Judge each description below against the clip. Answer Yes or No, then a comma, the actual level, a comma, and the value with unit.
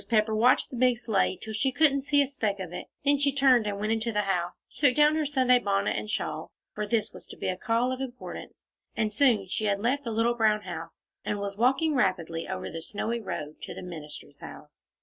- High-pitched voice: Yes, high, 225 Hz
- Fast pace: Yes, fast, 230 wpm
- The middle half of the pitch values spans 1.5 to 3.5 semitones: No, average, 4.4 semitones